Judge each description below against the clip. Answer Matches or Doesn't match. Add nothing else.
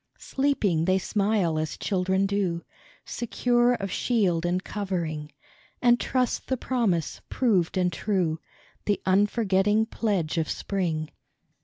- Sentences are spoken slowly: Matches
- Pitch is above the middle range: Matches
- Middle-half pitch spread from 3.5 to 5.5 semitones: Matches